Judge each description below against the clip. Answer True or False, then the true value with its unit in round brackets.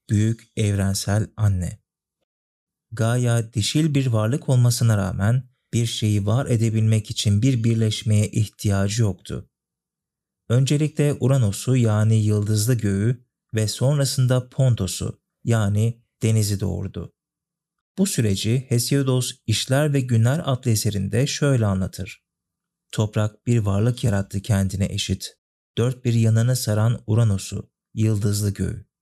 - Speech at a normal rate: True (110 wpm)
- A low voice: True (115 Hz)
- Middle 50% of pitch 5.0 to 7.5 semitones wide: False (3.3 semitones)